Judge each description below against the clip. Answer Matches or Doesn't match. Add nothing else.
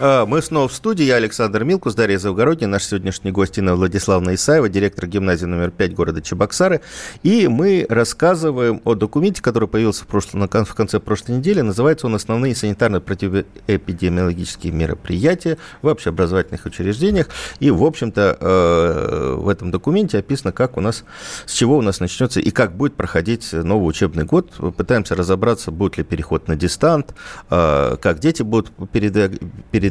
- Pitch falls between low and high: Doesn't match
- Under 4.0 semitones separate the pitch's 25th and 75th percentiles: Doesn't match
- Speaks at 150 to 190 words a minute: Matches